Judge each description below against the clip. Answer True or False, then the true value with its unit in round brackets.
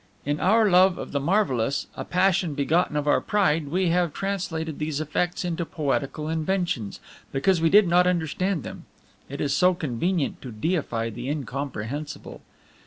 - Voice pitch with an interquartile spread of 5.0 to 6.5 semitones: False (4.3 semitones)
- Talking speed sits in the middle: True (160 wpm)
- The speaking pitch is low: False (160 Hz)